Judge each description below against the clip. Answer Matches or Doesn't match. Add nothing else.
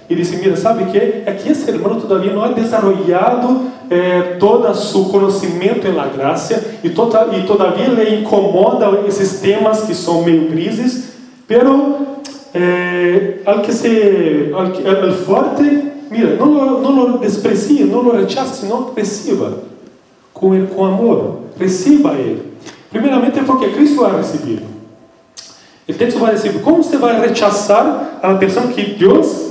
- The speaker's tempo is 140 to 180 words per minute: Matches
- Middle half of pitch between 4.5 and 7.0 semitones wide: Matches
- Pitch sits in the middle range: Doesn't match